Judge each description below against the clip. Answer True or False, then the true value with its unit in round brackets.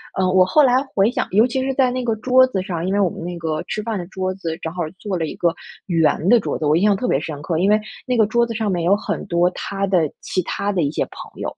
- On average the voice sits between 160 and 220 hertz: True (190 Hz)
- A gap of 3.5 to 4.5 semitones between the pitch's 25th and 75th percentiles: True (4.2 semitones)